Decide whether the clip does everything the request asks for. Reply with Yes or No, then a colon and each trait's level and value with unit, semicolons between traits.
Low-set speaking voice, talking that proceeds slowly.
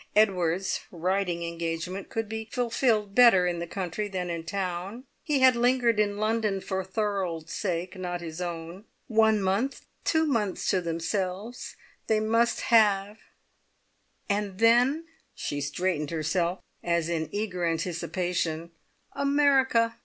No: high, 195 Hz; slow, 130 wpm